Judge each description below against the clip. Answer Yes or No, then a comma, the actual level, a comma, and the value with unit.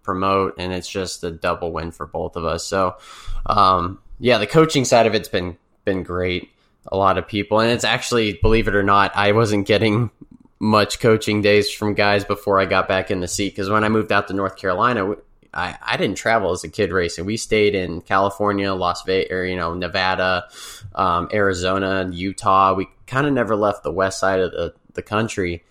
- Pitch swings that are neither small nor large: No, narrow, 2.3 semitones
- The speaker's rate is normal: No, fast, 210 wpm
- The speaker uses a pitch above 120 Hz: No, very low, 95 Hz